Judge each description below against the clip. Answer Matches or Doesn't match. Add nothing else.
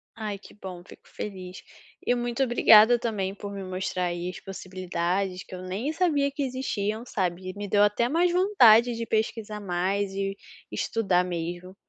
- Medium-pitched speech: Doesn't match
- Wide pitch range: Doesn't match